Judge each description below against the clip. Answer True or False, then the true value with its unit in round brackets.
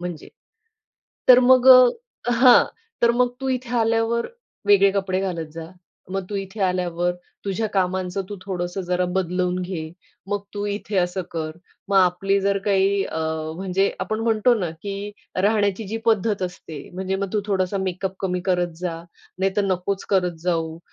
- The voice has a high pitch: True (195 Hz)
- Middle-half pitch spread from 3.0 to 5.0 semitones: False (2.5 semitones)